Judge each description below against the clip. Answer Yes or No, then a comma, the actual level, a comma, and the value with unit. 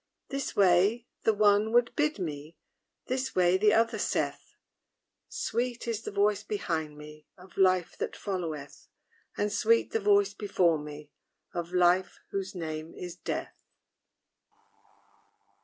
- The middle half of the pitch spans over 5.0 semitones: No, average, 4.1 semitones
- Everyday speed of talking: No, slow, 130 wpm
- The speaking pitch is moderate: No, high, 195 Hz